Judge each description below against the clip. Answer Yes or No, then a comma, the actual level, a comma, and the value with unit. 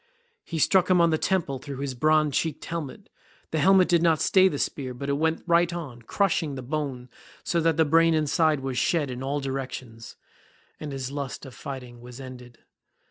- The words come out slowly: No, average, 195 wpm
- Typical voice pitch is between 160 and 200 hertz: No, medium, 145 Hz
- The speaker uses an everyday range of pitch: Yes, average, 4.0 semitones